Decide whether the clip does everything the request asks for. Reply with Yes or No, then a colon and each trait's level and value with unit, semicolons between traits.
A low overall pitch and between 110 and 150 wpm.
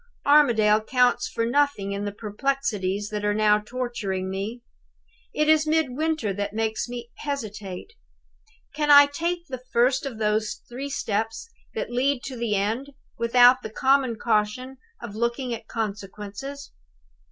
No: high, 235 Hz; average, 145 wpm